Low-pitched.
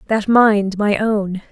No: high, 205 Hz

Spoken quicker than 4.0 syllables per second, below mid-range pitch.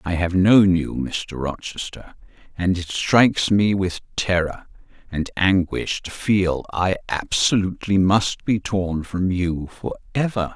No: 3.9 syllables/s; very low, 95 Hz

